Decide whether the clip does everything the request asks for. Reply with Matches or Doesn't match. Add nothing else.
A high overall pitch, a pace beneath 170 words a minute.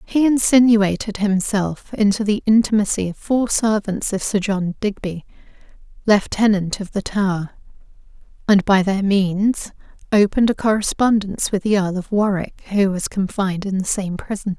Matches